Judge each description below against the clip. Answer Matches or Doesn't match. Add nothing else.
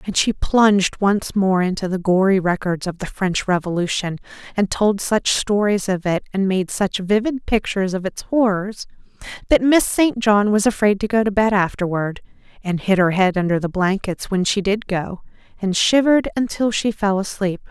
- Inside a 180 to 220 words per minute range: Matches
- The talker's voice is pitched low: Doesn't match